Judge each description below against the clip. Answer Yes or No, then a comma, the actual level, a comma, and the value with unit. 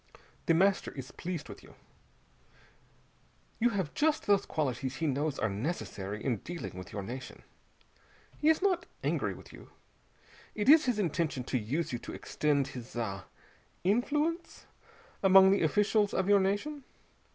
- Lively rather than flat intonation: Yes, wide, 8.2 semitones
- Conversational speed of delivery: Yes, average, 150 wpm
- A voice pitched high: No, medium, 170 Hz